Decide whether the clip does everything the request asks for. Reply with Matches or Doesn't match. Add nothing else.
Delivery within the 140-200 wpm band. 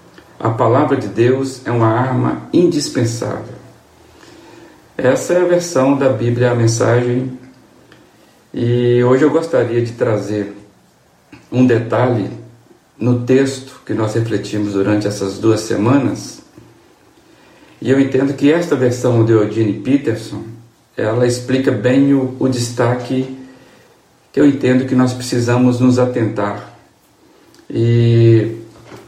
Doesn't match